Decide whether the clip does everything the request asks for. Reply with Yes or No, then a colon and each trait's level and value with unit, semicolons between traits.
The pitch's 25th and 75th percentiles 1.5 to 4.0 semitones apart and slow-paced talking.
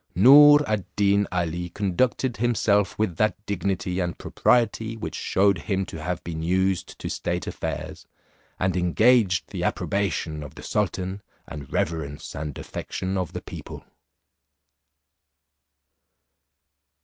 Yes: average, 3.4 semitones; slow, 125 wpm